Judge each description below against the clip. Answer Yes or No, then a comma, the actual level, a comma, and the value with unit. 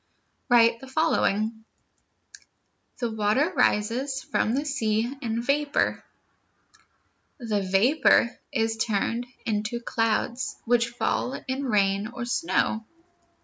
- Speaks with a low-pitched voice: No, high, 235 Hz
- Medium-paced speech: No, slow, 105 wpm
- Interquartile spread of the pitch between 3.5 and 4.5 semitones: No, average, 3.1 semitones